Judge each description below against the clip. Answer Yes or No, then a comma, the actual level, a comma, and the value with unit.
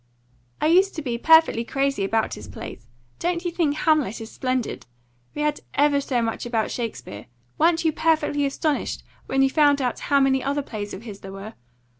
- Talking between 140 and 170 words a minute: No, average, 190 wpm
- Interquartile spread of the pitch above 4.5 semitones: Yes, average, 5.2 semitones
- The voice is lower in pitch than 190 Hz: No, very high, 275 Hz